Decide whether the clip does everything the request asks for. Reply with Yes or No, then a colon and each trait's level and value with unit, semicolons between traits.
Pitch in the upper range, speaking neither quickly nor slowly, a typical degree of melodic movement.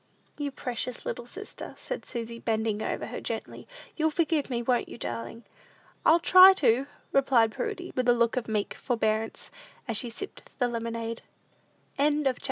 Yes: high, 245 Hz; average, 165 wpm; average, 4.3 semitones